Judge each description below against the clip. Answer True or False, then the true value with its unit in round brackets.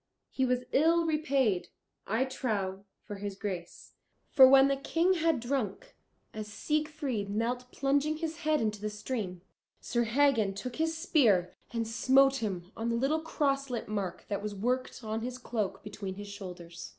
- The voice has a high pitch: True (240 Hz)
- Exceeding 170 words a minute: False (165 wpm)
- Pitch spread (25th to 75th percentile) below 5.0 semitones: False (5.3 semitones)